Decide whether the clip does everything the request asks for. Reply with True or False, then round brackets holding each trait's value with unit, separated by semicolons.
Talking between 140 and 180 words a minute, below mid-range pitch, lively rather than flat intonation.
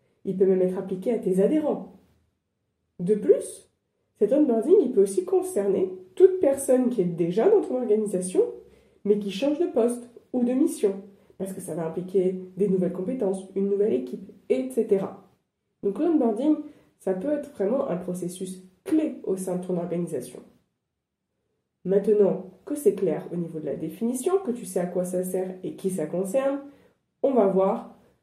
False (170 wpm; 205 Hz; 6.8 semitones)